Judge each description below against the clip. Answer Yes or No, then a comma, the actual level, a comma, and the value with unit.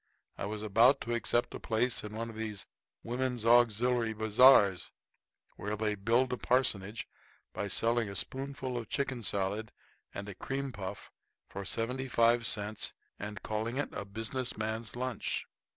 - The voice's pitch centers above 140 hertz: No, low, 115 Hz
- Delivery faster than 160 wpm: No, average, 155 wpm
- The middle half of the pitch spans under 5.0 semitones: Yes, average, 2.9 semitones